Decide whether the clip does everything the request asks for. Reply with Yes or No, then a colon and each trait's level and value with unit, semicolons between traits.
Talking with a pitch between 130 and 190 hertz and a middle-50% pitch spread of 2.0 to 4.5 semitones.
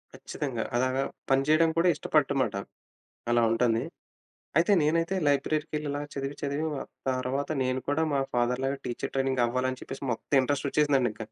Yes: low, 135 Hz; narrow, 2.4 semitones